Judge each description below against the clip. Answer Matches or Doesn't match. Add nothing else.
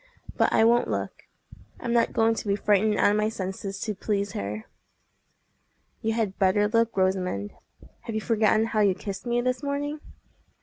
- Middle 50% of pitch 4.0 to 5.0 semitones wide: Doesn't match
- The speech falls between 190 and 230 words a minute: Doesn't match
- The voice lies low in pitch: Doesn't match